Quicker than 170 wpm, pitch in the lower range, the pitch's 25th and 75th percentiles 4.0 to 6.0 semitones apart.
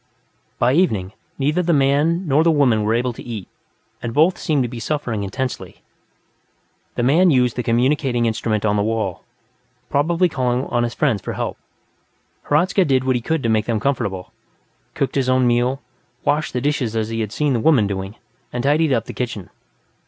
Yes: average, 190 wpm; low, 125 Hz; average, 4.4 semitones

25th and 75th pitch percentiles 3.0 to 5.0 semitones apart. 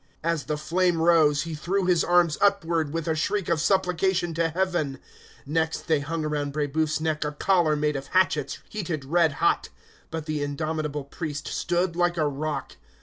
No: narrow, 2.6 semitones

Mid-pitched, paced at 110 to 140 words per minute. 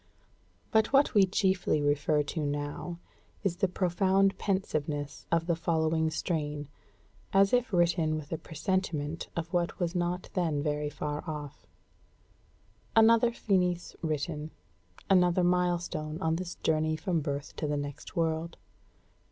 Yes: medium, 165 Hz; slow, 135 wpm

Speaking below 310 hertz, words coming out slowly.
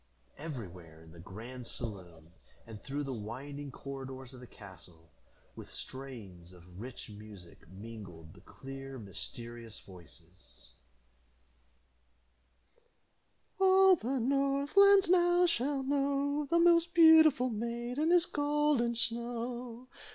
Yes: low, 135 Hz; slow, 110 wpm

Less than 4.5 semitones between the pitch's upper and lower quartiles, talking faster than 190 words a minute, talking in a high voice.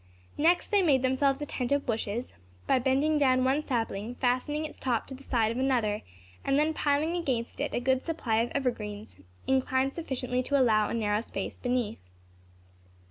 No: average, 3.3 semitones; average, 180 wpm; very high, 260 Hz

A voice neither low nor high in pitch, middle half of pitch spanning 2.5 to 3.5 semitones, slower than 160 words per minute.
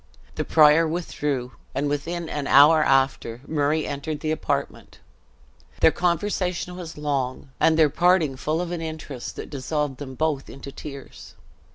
Yes: medium, 150 Hz; average, 2.8 semitones; average, 150 wpm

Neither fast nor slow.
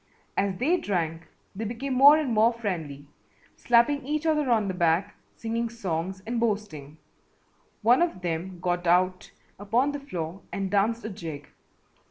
Yes: average, 155 wpm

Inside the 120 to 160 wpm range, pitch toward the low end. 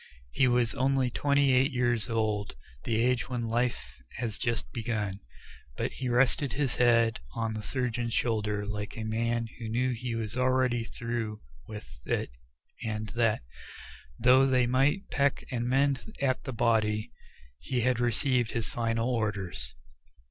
Yes: average, 150 wpm; low, 120 Hz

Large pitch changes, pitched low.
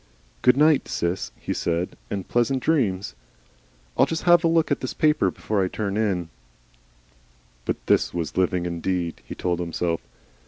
Yes: wide, 8.0 semitones; very low, 95 Hz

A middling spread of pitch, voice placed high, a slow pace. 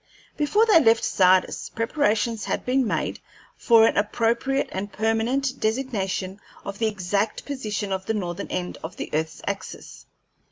No: average, 4.4 semitones; high, 220 Hz; average, 150 wpm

